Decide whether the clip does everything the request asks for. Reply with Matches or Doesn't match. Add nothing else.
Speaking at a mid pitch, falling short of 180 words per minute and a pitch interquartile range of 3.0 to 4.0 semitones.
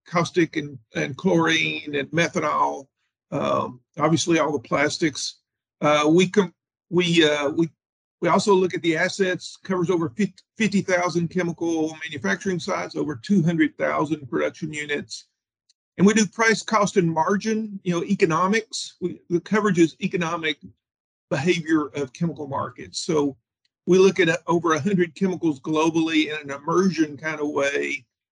Matches